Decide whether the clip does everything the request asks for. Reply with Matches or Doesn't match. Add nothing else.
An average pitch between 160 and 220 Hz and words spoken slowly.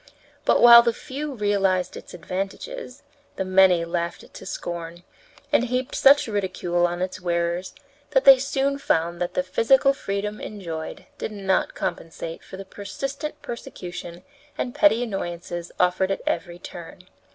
Doesn't match